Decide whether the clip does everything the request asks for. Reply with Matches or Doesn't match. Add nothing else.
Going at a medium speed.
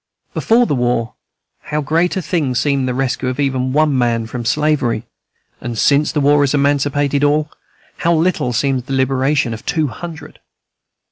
Matches